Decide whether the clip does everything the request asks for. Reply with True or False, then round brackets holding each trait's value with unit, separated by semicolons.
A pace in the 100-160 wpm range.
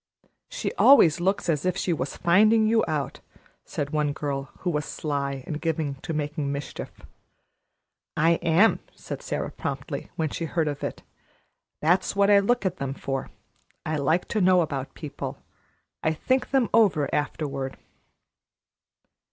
True (150 wpm)